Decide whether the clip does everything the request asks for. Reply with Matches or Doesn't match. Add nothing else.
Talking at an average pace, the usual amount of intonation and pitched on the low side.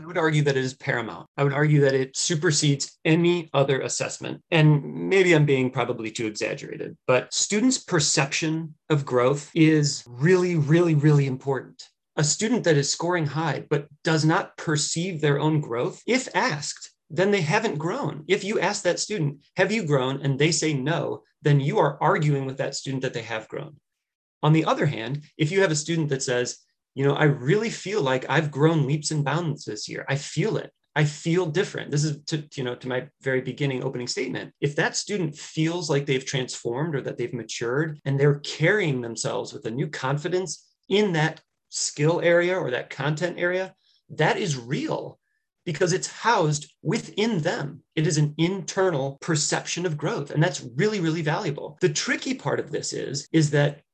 Doesn't match